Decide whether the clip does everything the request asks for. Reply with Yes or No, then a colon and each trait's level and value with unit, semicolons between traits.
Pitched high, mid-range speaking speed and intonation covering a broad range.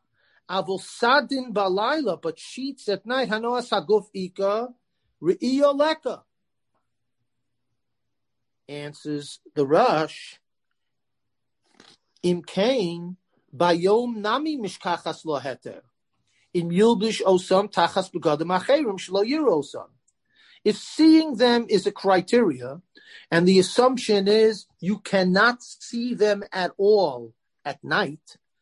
No: high, 195 Hz; slow, 90 wpm; wide, 5.7 semitones